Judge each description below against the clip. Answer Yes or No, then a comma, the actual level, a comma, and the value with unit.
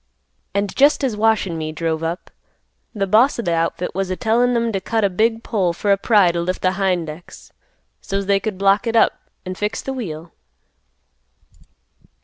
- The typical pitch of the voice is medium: No, high, 195 Hz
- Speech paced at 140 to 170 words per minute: No, average, 195 wpm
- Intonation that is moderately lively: Yes, average, 4.0 semitones